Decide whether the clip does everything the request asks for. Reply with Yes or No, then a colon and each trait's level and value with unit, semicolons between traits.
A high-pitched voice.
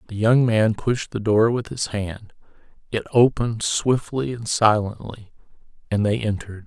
No: low, 110 Hz